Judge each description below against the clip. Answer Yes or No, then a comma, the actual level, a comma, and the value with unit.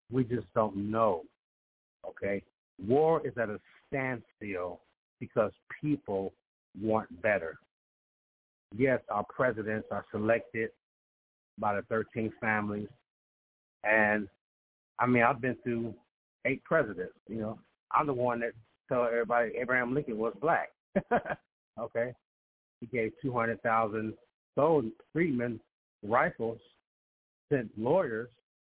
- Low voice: Yes, low, 110 Hz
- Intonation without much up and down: No, average, 3.3 semitones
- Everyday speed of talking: No, slow, 110 wpm